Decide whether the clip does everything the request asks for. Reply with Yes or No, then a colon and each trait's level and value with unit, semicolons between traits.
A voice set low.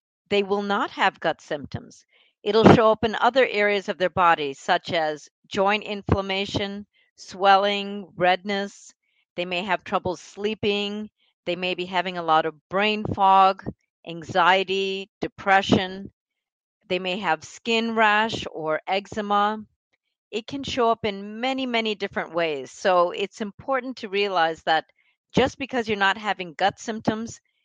No: high, 200 Hz